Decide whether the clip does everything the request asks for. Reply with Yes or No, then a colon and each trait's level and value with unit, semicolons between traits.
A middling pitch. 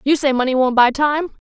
No: very high, 275 Hz